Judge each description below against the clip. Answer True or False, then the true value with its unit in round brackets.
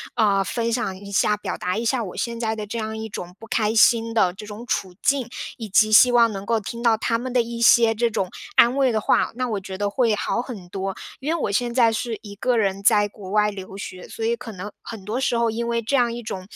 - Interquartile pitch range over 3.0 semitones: False (2.7 semitones)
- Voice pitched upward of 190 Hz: True (225 Hz)